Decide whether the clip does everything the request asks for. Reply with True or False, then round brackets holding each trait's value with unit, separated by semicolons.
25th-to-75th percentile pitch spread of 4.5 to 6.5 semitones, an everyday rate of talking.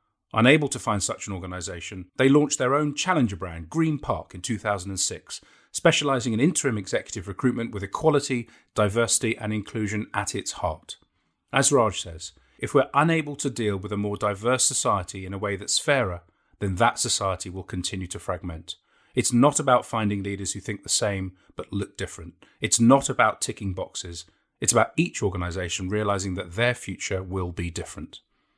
True (5.1 semitones; 170 wpm)